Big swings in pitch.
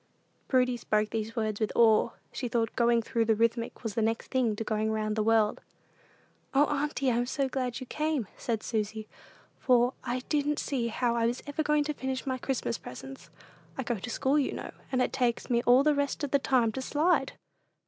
No: average, 3.2 semitones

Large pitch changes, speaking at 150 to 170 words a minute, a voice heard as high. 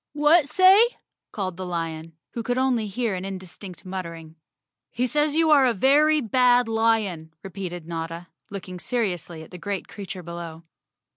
Yes: wide, 6.4 semitones; average, 155 wpm; high, 195 Hz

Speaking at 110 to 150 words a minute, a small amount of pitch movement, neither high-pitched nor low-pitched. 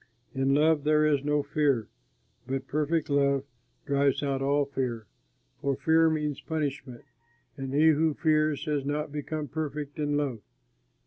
Yes: average, 145 wpm; narrow, 1.8 semitones; medium, 145 Hz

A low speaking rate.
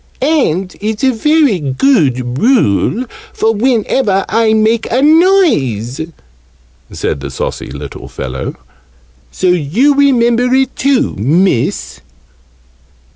Yes: slow, 105 wpm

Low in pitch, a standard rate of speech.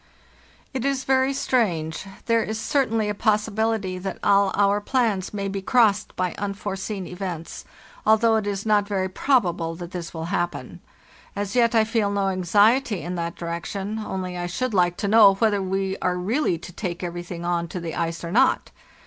No: high, 200 Hz; average, 185 wpm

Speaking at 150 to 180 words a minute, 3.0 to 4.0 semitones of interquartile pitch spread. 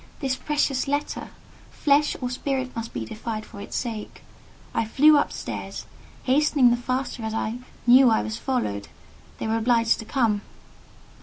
Yes: average, 160 wpm; average, 3.5 semitones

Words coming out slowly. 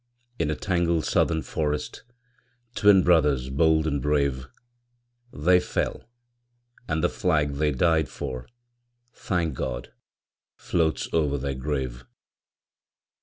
Yes: slow, 110 wpm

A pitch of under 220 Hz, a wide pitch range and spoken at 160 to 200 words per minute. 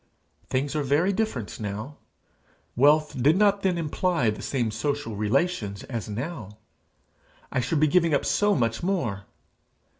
No: medium, 140 Hz; wide, 7.1 semitones; average, 145 wpm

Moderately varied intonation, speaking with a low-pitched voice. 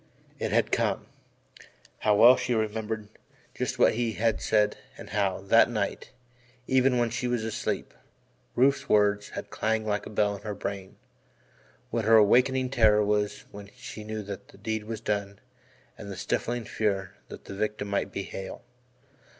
No: narrow, 1.9 semitones; low, 105 Hz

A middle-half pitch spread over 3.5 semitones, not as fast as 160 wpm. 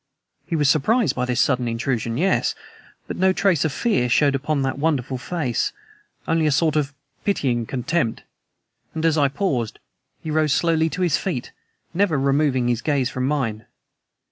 No: average, 4.4 semitones; average, 170 wpm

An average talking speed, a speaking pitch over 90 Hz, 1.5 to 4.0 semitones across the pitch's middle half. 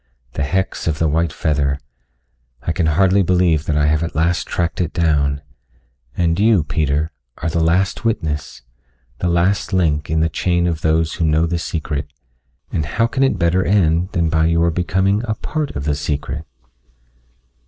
No: average, 175 wpm; very low, 85 Hz; average, 2.8 semitones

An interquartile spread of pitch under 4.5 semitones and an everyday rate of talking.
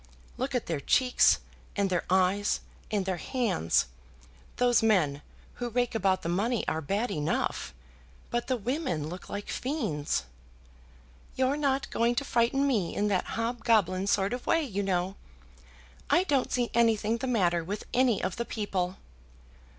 No: average, 4.9 semitones; average, 155 wpm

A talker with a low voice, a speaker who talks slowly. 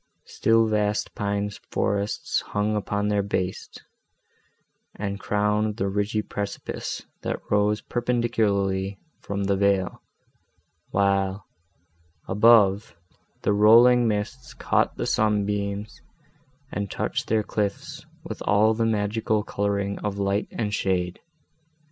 Yes: low, 105 Hz; slow, 110 wpm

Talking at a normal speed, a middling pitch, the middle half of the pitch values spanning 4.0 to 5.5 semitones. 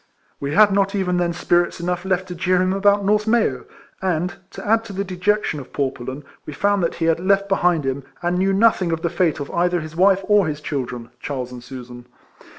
No: fast, 225 wpm; medium, 175 Hz; average, 4.5 semitones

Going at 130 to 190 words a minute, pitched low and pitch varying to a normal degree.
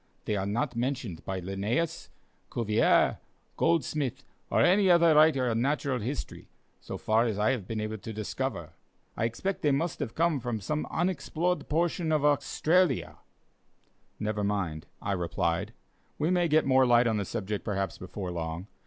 No: average, 160 wpm; low, 120 Hz; wide, 6.8 semitones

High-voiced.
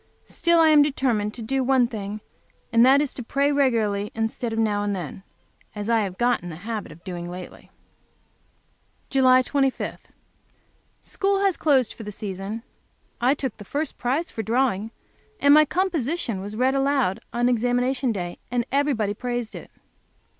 Yes: high, 240 Hz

